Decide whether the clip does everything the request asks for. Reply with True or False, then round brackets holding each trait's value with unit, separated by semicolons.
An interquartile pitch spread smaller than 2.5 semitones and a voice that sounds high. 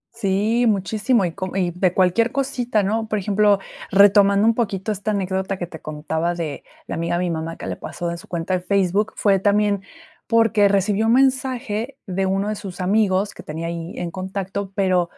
False (2.9 semitones; 195 Hz)